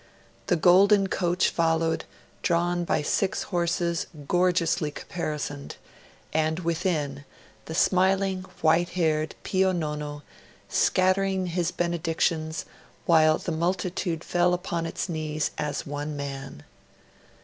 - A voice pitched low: No, medium, 170 Hz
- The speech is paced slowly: Yes, slow, 105 wpm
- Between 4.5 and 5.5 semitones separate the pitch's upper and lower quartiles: No, narrow, 2.4 semitones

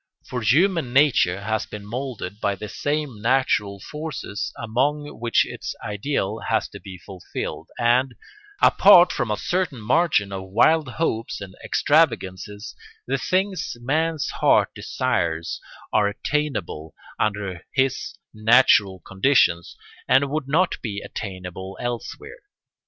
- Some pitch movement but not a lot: No, wide, 6.5 semitones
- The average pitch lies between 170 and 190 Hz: No, low, 115 Hz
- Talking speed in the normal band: No, slow, 125 wpm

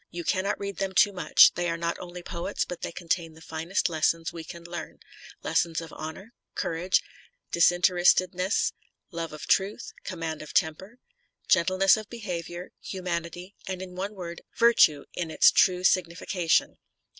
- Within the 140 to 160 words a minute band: Yes, average, 155 wpm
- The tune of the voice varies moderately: No, narrow, 2.1 semitones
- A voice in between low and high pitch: Yes, medium, 175 Hz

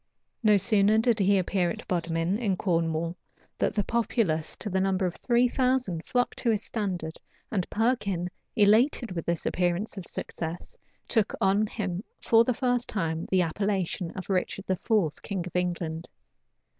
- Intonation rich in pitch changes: No, average, 4.1 semitones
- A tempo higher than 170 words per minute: No, average, 160 wpm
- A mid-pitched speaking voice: No, high, 195 Hz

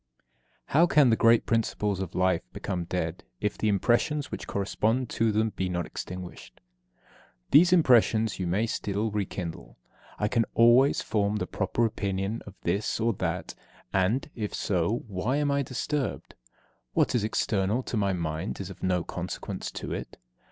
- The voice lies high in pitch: No, low, 105 Hz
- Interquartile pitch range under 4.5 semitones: Yes, average, 4.0 semitones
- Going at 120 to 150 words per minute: No, average, 165 wpm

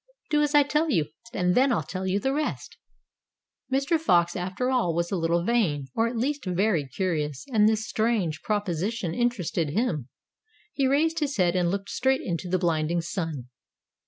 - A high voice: Yes, high, 195 Hz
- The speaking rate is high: No, average, 180 wpm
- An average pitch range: No, wide, 6.6 semitones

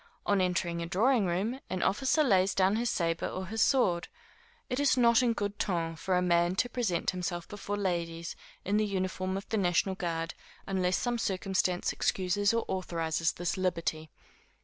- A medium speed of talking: Yes, average, 175 wpm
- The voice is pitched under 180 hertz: No, medium, 185 Hz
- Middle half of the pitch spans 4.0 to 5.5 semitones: No, average, 3.1 semitones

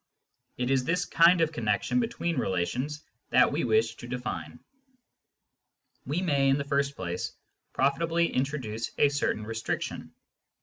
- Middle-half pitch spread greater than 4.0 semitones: Yes, average, 5.0 semitones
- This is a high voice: No, medium, 140 Hz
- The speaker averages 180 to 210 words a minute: No, slow, 135 wpm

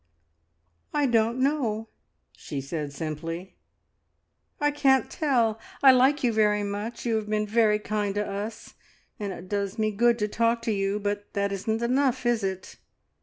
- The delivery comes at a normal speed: Yes, average, 165 wpm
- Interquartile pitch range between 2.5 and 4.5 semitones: Yes, average, 3.0 semitones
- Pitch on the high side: Yes, high, 215 Hz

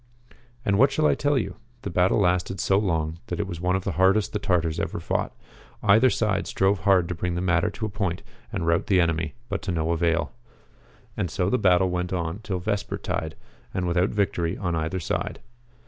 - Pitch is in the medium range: No, very low, 90 Hz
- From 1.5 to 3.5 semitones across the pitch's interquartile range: Yes, average, 3.0 semitones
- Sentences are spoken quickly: Yes, fast, 210 wpm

